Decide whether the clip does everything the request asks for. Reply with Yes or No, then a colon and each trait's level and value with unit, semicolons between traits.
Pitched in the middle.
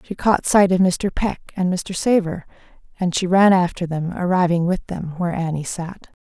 Yes: medium, 180 Hz